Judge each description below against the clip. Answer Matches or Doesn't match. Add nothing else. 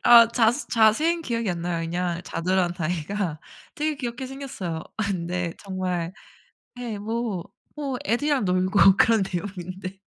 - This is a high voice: Matches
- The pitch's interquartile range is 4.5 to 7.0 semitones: Matches